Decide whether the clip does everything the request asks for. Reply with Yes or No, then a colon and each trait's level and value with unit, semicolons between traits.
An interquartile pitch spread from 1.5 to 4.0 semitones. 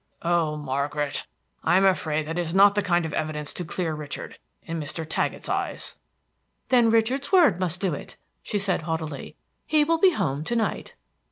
No: average, 5.1 semitones